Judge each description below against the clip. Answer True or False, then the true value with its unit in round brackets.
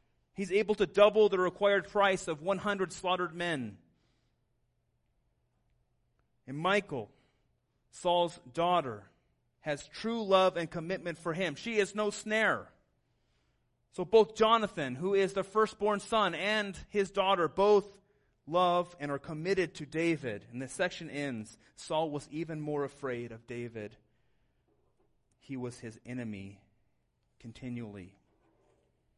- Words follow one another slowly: True (125 wpm)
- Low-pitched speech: False (170 Hz)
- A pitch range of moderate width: False (8.3 semitones)